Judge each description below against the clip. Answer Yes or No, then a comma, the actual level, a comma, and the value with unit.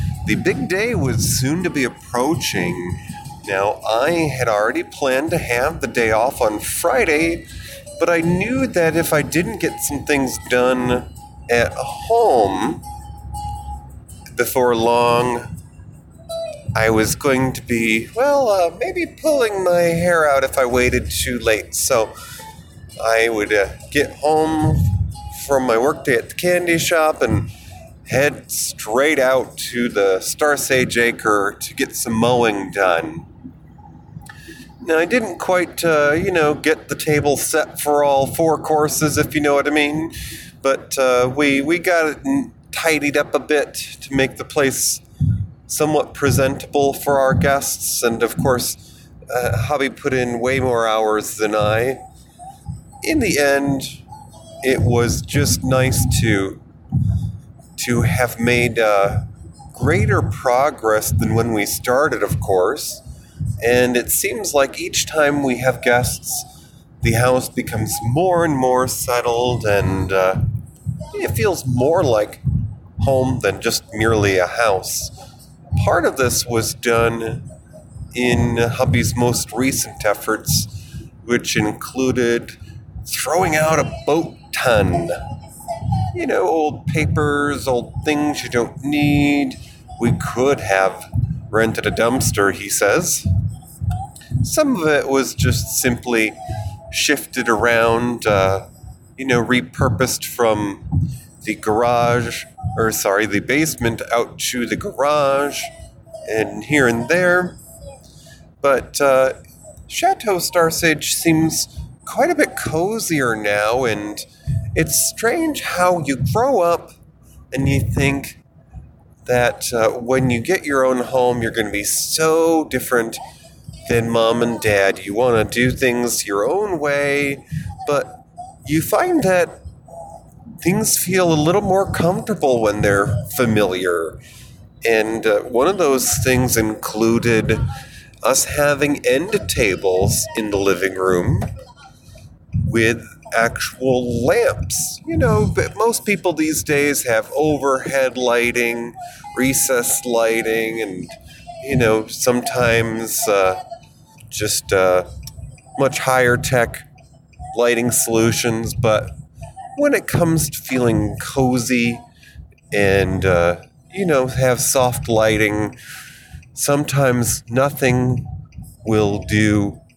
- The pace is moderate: No, slow, 125 wpm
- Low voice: Yes, low, 125 Hz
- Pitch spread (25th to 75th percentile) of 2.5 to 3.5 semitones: No, average, 4.6 semitones